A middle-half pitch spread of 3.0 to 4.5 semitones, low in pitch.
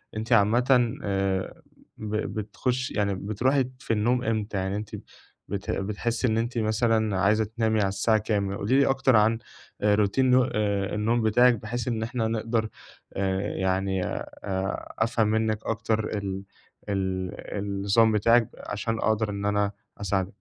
No: narrow, 2.4 semitones; low, 110 Hz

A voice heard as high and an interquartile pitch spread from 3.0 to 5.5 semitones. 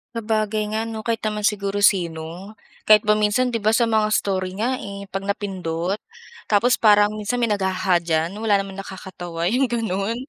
No: high, 205 Hz; narrow, 2.5 semitones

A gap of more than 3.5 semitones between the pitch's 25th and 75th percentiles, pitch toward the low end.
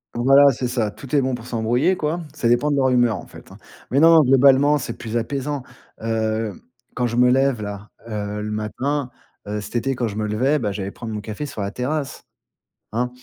Yes: average, 4.1 semitones; low, 125 Hz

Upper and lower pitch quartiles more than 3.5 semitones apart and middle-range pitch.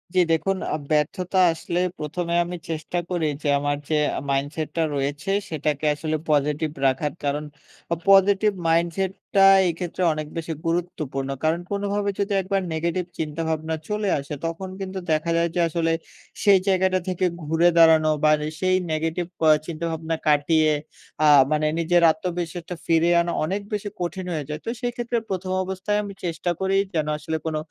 No: average, 3.2 semitones; medium, 165 Hz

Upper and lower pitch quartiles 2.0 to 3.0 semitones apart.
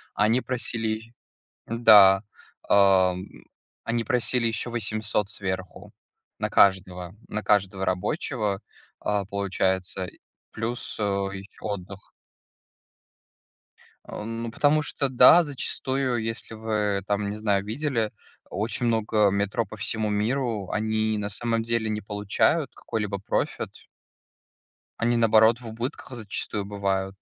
Yes: average, 2.7 semitones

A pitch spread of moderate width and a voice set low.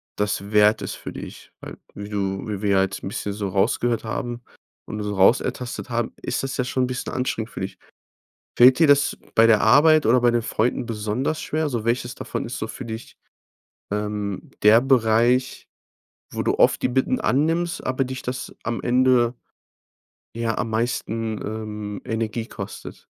Yes: average, 3.2 semitones; low, 115 Hz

